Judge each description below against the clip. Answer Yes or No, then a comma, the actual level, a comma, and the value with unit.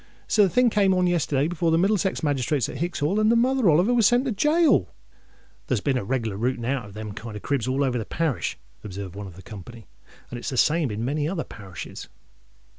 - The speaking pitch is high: No, medium, 140 Hz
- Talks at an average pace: No, fast, 230 wpm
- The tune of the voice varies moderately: No, wide, 8.9 semitones